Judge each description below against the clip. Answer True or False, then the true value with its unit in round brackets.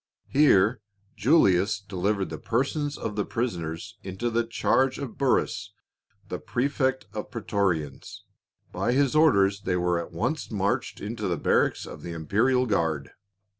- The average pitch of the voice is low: True (105 Hz)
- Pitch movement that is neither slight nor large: False (5.9 semitones)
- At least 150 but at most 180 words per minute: False (140 wpm)